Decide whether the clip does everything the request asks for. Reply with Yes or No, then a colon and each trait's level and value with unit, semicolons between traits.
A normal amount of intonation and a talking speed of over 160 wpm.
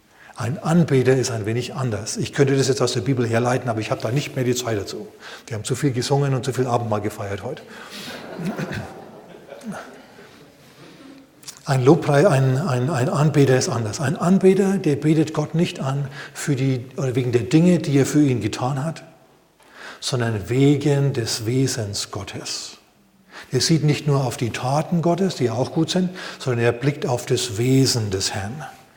Yes: average, 3.7 semitones; average, 180 wpm